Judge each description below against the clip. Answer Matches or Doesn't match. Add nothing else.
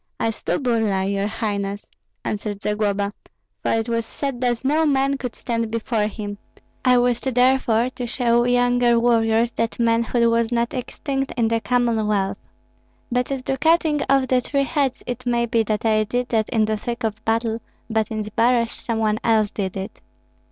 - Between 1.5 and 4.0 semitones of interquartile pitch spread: Matches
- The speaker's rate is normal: Matches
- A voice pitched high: Matches